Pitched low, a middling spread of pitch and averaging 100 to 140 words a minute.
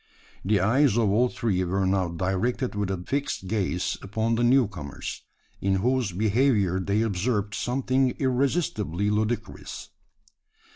Yes: low, 105 Hz; average, 4.4 semitones; slow, 135 wpm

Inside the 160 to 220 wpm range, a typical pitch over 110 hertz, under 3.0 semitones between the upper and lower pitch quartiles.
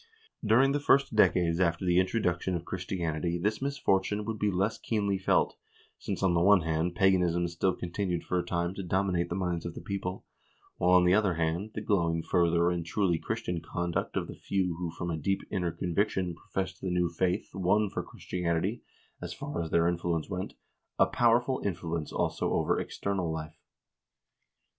No: average, 180 wpm; very low, 90 Hz; narrow, 2.4 semitones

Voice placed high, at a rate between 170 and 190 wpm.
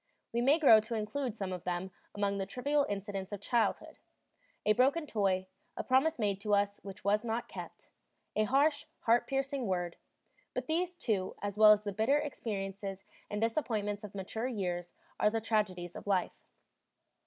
Yes: high, 210 Hz; average, 175 wpm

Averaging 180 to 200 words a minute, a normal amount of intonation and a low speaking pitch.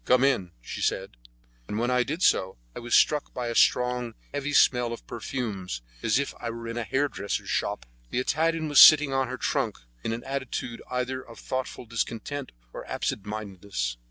Yes: average, 185 wpm; average, 3.0 semitones; low, 125 Hz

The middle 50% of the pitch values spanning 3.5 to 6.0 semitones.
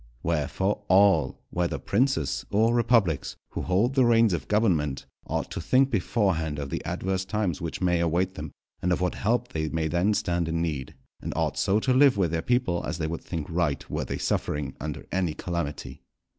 Yes: average, 5.0 semitones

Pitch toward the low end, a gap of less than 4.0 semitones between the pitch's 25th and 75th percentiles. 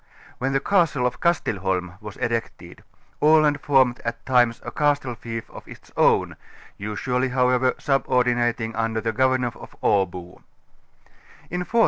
Yes: low, 125 Hz; average, 2.8 semitones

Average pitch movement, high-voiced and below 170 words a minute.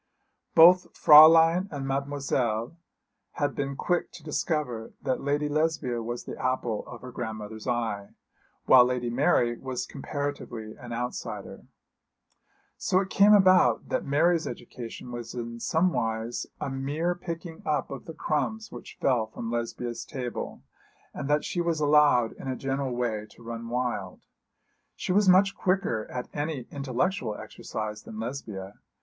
No: average, 4.9 semitones; low, 135 Hz; average, 145 wpm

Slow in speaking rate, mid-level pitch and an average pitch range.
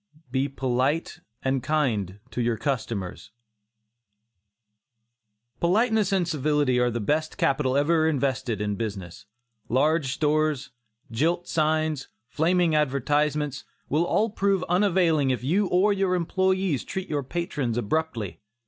Yes: slow, 120 wpm; medium, 150 Hz; average, 4.9 semitones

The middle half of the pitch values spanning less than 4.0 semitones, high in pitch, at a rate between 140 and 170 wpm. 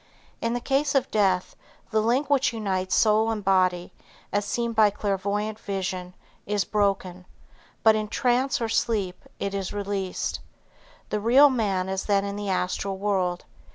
Yes: average, 2.8 semitones; high, 205 Hz; average, 155 wpm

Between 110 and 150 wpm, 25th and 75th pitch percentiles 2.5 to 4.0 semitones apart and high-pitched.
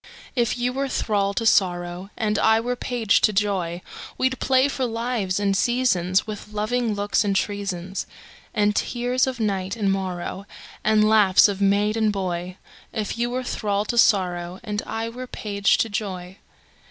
Yes: average, 140 wpm; average, 3.2 semitones; high, 210 Hz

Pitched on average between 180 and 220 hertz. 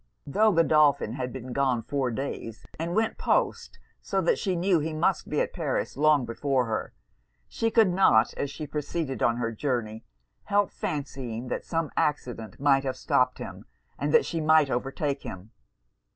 No: medium, 140 Hz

